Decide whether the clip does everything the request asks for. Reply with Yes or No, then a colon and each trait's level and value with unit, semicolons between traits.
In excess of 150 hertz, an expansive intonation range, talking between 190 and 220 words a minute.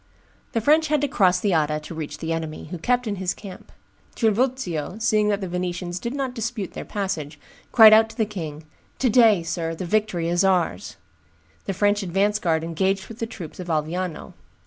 No: high, 190 Hz; average, 4.8 semitones; average, 195 wpm